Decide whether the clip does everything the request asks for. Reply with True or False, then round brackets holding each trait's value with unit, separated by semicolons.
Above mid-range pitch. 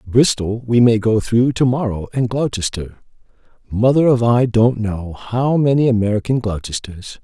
False (115 Hz)